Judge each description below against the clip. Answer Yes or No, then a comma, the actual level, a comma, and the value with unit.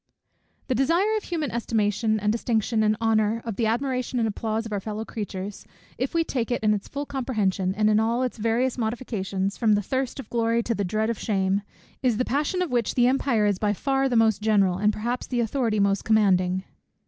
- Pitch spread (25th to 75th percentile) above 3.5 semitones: No, average, 3.1 semitones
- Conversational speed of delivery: No, fast, 220 wpm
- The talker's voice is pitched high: Yes, high, 225 Hz